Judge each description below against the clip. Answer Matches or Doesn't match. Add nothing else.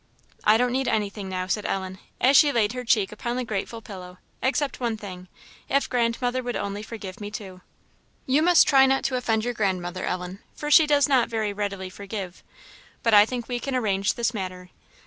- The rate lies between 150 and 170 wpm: Doesn't match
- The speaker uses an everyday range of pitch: Matches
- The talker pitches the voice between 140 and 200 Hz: Doesn't match